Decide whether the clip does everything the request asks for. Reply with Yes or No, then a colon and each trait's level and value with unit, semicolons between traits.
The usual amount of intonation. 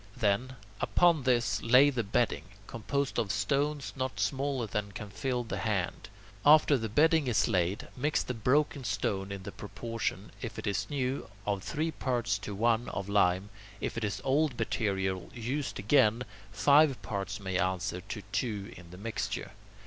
Yes: average, 5.0 semitones